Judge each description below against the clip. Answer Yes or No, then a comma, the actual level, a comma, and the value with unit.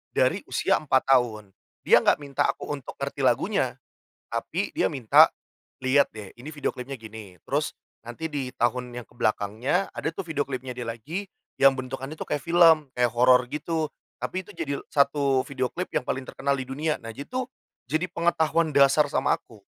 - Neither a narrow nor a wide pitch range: Yes, average, 3.8 semitones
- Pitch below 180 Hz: Yes, low, 135 Hz